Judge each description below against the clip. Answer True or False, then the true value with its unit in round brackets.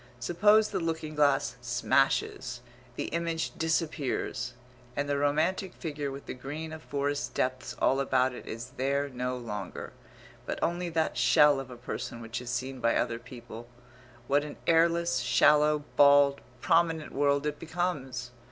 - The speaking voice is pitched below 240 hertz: True (140 Hz)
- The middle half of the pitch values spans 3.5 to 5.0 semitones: True (4.0 semitones)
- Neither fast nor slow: True (150 wpm)